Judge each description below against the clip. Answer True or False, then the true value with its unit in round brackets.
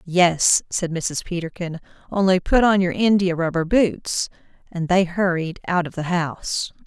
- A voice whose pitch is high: False (175 Hz)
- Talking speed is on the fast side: False (155 wpm)